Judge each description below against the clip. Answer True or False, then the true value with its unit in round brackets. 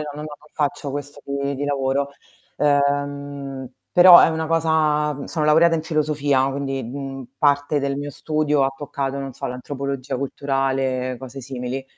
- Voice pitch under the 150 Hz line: True (140 Hz)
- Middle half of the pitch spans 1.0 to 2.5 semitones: True (1.7 semitones)